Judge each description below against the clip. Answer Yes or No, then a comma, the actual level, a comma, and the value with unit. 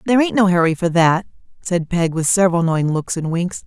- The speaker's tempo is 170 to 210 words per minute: No, fast, 230 wpm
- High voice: No, medium, 175 Hz